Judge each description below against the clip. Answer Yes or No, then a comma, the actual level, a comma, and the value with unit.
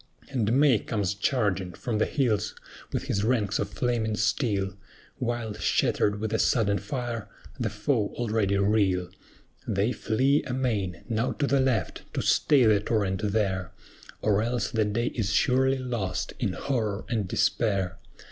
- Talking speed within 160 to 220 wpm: No, average, 150 wpm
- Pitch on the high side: No, low, 110 Hz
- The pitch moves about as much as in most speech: Yes, average, 3.4 semitones